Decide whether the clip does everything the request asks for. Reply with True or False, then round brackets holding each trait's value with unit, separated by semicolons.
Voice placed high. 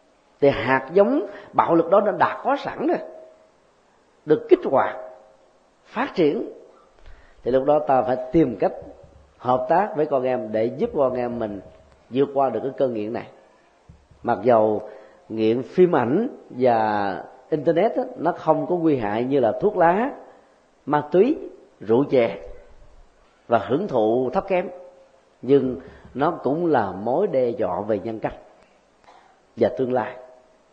False (135 Hz)